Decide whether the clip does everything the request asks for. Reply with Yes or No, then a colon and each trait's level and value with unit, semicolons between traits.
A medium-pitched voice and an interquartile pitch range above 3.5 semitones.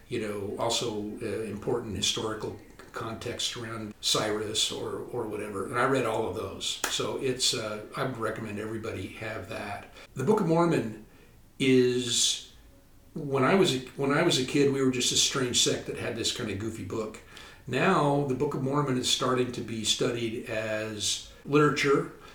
No: low, 120 Hz; average, 3.9 semitones